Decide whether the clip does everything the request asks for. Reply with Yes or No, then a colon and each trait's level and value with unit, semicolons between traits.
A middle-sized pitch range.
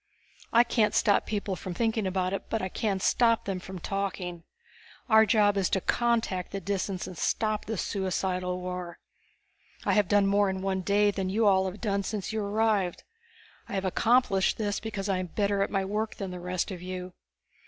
No: narrow, 2.2 semitones